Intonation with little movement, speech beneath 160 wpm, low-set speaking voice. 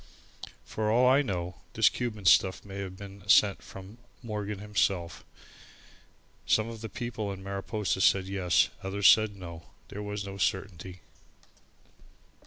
Yes: narrow, 2.1 semitones; average, 140 wpm; low, 100 Hz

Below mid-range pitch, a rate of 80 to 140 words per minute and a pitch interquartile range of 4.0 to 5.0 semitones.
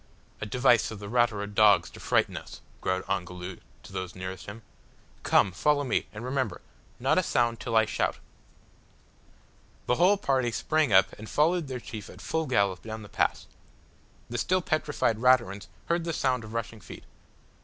No: low, 115 Hz; average, 175 wpm; average, 4.6 semitones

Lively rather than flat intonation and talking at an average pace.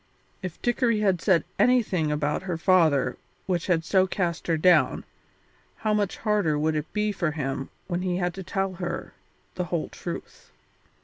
No: average, 3.2 semitones; average, 170 wpm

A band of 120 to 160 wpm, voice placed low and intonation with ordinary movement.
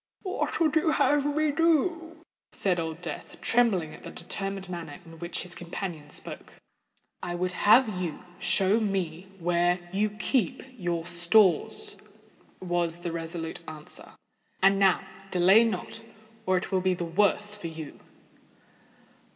No: slow, 135 wpm; medium, 185 Hz; average, 4.2 semitones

